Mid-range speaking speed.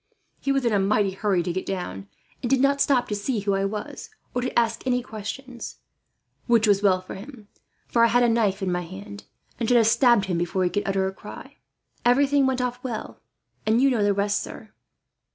No: fast, 225 wpm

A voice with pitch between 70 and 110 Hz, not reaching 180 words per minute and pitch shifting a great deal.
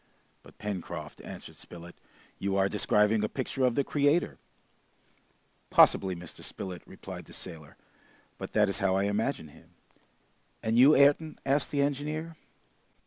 Yes: low, 105 Hz; average, 140 wpm; wide, 6.8 semitones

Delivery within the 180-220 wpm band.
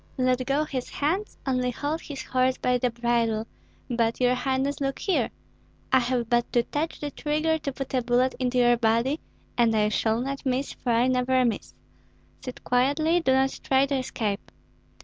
Yes: average, 185 wpm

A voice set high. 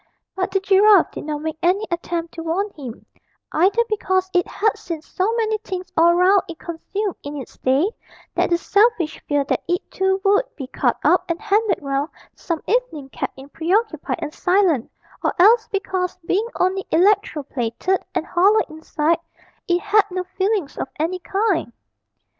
Yes: very high, 365 Hz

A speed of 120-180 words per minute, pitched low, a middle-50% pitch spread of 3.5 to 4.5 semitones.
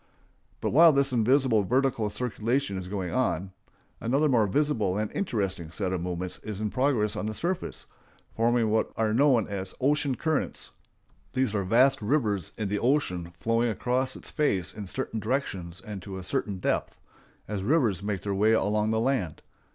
No: average, 175 wpm; low, 110 Hz; average, 5.0 semitones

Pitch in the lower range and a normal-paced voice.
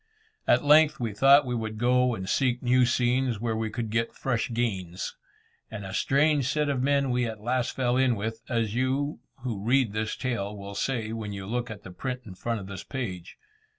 No: low, 120 Hz; fast, 210 wpm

